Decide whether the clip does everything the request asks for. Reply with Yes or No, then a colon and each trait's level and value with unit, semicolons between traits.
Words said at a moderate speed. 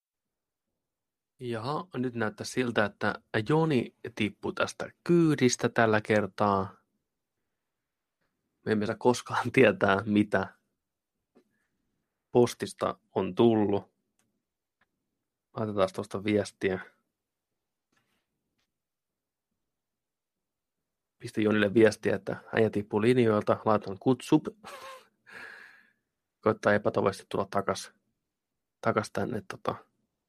No: slow, 75 wpm